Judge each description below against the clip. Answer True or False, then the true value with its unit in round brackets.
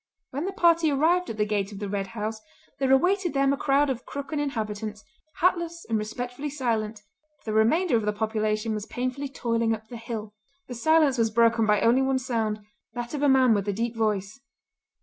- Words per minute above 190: True (200 wpm)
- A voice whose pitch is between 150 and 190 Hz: False (235 Hz)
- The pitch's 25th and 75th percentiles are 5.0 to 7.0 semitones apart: False (4.4 semitones)